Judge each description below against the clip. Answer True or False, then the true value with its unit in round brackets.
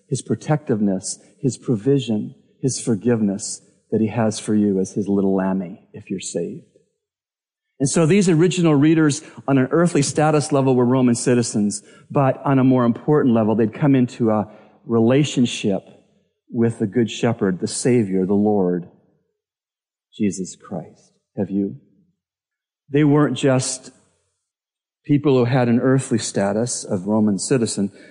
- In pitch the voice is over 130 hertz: False (120 Hz)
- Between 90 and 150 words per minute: True (140 wpm)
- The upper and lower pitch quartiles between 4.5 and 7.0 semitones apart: True (4.9 semitones)